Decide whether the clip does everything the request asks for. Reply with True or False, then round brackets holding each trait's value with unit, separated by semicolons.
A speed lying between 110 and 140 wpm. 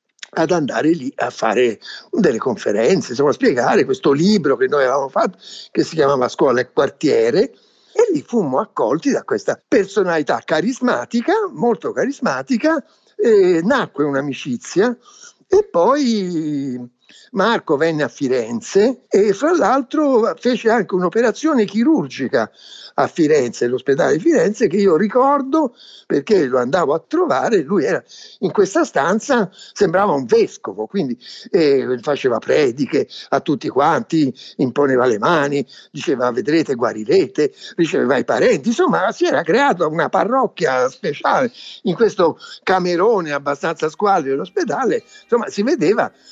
True (130 wpm)